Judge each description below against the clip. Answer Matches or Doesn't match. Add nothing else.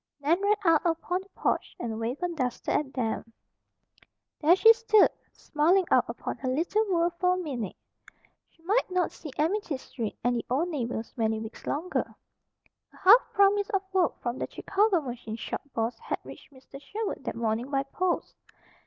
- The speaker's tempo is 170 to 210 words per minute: Matches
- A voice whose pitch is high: Matches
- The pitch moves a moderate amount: Doesn't match